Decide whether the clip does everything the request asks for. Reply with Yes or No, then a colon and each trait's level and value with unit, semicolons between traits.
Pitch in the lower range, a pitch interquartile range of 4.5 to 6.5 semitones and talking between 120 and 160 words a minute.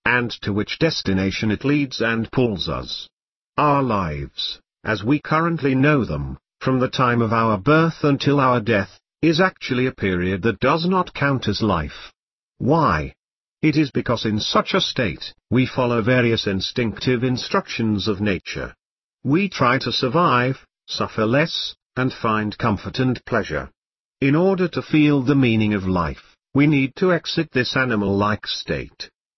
Yes: low, 125 Hz; average, 5.2 semitones; average, 155 wpm